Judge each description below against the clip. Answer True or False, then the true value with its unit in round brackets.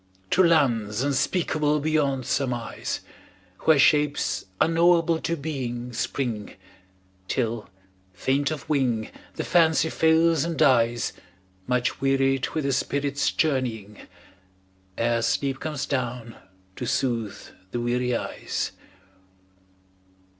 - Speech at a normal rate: False (105 wpm)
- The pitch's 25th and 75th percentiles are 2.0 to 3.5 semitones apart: False (4.2 semitones)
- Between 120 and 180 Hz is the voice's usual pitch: True (135 Hz)